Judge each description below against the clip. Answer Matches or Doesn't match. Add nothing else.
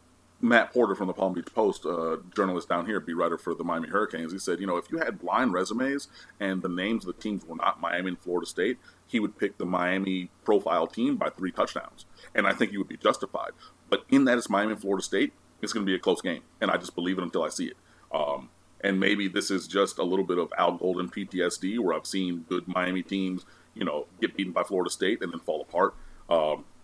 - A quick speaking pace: Matches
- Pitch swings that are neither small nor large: Doesn't match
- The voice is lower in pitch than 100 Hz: Matches